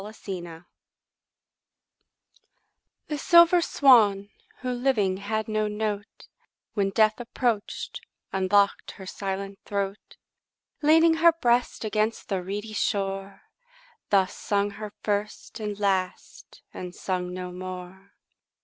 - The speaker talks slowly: Yes, slow, 110 wpm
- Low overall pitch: No, high, 205 Hz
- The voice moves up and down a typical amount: No, narrow, 2.3 semitones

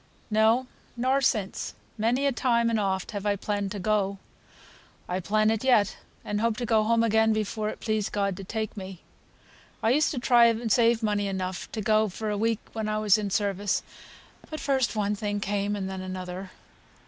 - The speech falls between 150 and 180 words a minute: No, average, 195 wpm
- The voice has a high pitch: Yes, high, 215 Hz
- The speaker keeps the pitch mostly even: Yes, narrow, 2.3 semitones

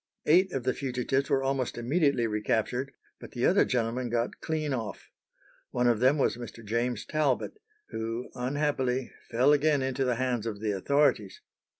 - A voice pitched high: No, low, 125 Hz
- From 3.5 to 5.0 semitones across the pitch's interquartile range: No, average, 3.1 semitones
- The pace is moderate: Yes, average, 165 wpm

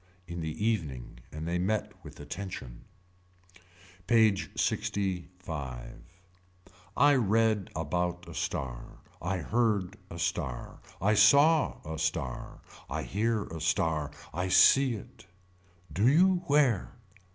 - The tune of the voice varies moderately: No, wide, 5.7 semitones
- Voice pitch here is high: No, very low, 95 Hz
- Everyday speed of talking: No, slow, 115 wpm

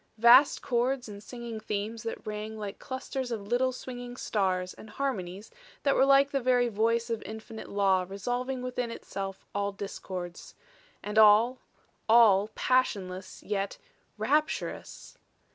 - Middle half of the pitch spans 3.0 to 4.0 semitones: Yes, average, 3.6 semitones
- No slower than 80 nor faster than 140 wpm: Yes, slow, 135 wpm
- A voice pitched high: Yes, high, 225 Hz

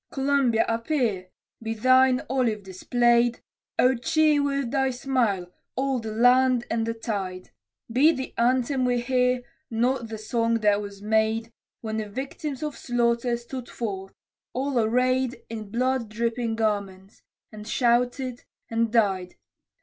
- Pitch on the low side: No, high, 235 Hz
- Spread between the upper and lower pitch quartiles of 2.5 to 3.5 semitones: Yes, average, 2.8 semitones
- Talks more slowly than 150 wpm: Yes, slow, 135 wpm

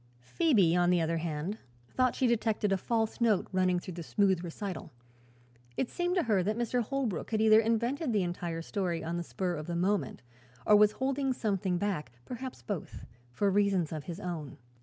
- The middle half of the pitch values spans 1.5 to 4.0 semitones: No, average, 4.7 semitones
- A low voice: No, high, 200 Hz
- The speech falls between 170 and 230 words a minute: Yes, average, 190 wpm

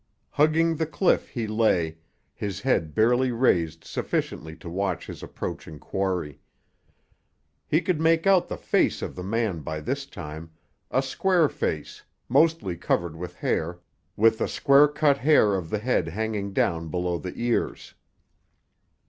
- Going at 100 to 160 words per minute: Yes, average, 150 wpm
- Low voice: Yes, low, 105 Hz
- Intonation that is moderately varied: No, wide, 8.5 semitones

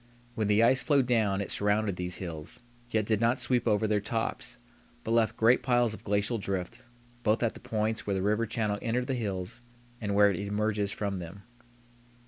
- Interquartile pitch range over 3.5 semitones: No, narrow, 2.4 semitones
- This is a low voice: Yes, low, 105 Hz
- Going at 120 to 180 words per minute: No, average, 195 wpm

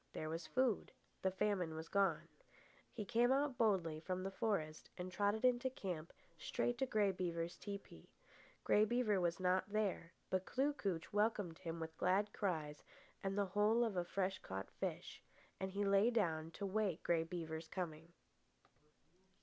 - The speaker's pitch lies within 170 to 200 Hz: Yes, high, 190 Hz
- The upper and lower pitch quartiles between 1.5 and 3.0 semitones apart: No, average, 4.1 semitones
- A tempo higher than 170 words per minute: No, average, 165 wpm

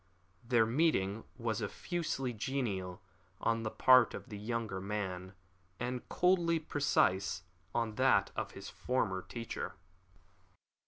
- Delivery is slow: Yes, slow, 115 wpm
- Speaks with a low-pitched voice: Yes, low, 115 Hz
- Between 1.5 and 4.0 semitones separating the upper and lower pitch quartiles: No, average, 4.6 semitones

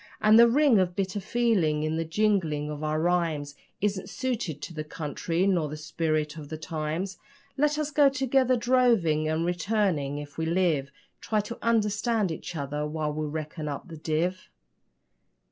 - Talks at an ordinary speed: Yes, average, 170 wpm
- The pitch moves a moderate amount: No, wide, 5.7 semitones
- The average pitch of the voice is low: No, medium, 170 Hz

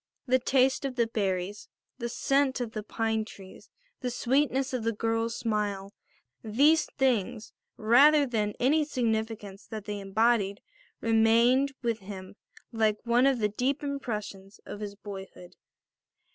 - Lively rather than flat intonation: No, average, 3.7 semitones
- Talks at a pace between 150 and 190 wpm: No, average, 140 wpm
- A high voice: Yes, high, 225 Hz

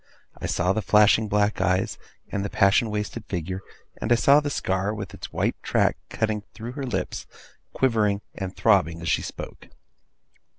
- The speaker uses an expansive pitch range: No, narrow, 2.5 semitones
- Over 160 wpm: Yes, average, 170 wpm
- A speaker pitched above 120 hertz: No, low, 105 Hz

